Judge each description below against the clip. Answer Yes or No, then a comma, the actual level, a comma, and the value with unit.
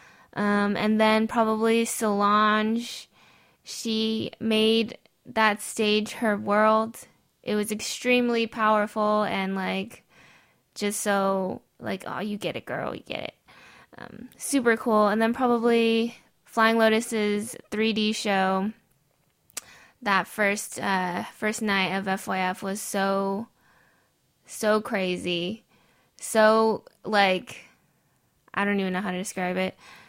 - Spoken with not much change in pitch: Yes, narrow, 2.2 semitones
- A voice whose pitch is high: Yes, high, 215 Hz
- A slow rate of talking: Yes, slow, 120 wpm